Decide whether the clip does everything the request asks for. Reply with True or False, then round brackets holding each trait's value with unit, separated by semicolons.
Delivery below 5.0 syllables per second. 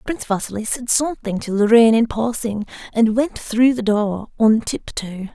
True (4.8 syllables/s)